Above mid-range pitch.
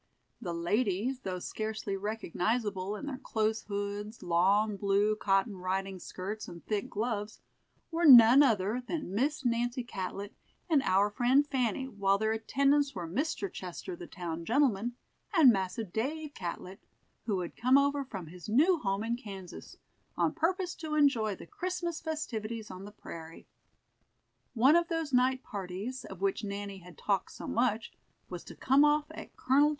Yes: high, 220 Hz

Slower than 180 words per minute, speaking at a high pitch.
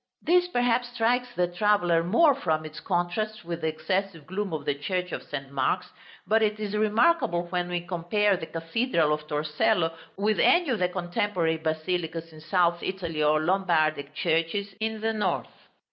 No: average, 170 wpm; medium, 180 Hz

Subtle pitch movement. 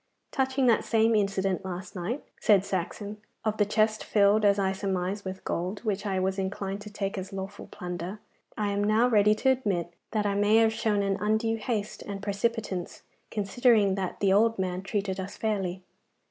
Yes: narrow, 2.2 semitones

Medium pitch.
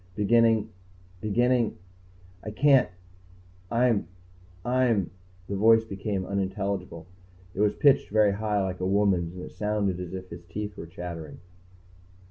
No: low, 100 Hz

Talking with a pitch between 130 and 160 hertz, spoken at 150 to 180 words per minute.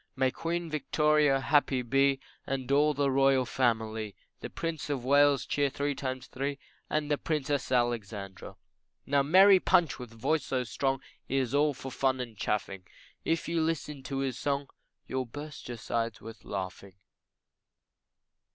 Yes: low, 135 Hz; average, 155 wpm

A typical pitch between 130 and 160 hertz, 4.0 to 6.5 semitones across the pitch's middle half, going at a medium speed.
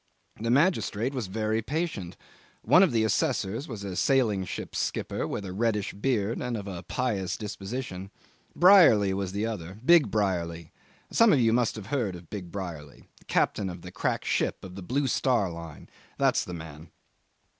No: low, 105 Hz; average, 5.0 semitones; average, 175 wpm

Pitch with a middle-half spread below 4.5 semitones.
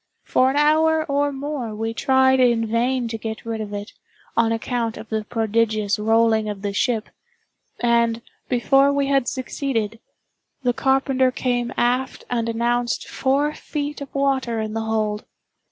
Yes: average, 3.1 semitones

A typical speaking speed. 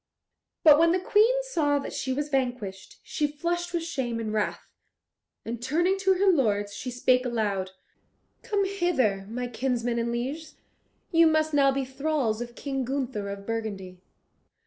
Yes: average, 160 wpm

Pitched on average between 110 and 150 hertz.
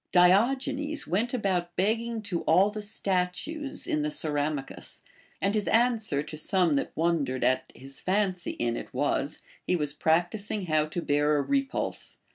No: medium, 185 Hz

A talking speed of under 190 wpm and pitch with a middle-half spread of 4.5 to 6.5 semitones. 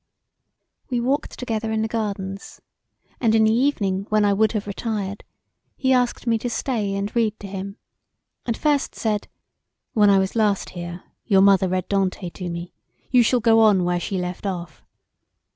No: average, 175 wpm; average, 2.9 semitones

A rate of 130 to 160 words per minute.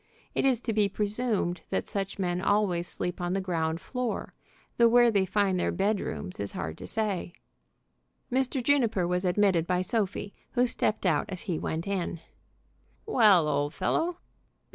No: average, 170 wpm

